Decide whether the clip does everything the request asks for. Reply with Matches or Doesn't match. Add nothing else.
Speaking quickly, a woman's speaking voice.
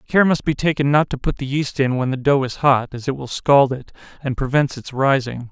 Doesn't match